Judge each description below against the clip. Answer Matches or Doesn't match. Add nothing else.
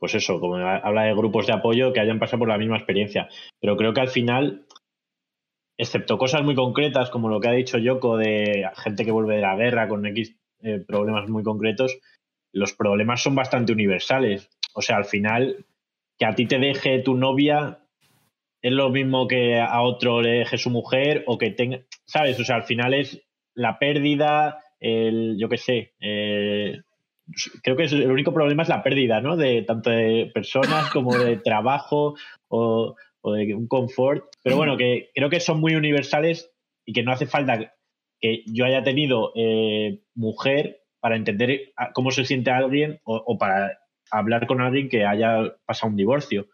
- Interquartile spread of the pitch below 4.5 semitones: Matches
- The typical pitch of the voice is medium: Doesn't match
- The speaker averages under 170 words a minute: Doesn't match